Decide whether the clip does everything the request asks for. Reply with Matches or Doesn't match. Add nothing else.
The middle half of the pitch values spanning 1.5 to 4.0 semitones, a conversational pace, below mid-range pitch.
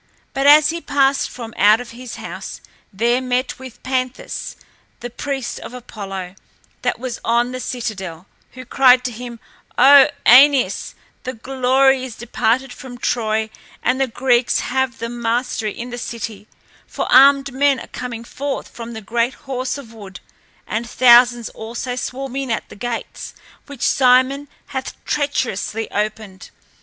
Doesn't match